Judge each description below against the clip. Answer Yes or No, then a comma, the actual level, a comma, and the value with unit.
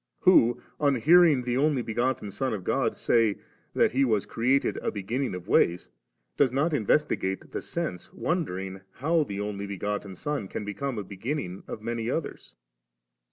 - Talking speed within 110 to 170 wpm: Yes, average, 165 wpm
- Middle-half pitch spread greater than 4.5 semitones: Yes, wide, 5.6 semitones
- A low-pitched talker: Yes, low, 120 Hz